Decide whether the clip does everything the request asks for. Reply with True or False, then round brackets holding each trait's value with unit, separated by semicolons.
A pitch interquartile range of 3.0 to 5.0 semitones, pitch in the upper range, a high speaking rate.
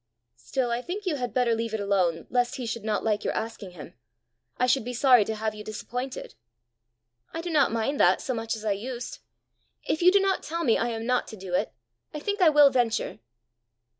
True (3.8 semitones; 240 Hz; 225 wpm)